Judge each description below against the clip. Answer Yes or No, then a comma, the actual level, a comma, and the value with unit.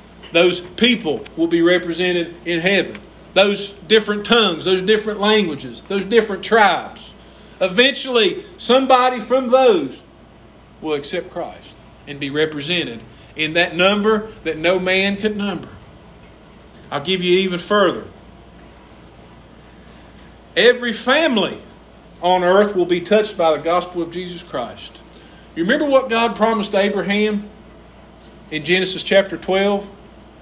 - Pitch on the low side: No, high, 190 Hz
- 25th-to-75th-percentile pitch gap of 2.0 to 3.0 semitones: No, average, 3.8 semitones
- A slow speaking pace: Yes, slow, 120 wpm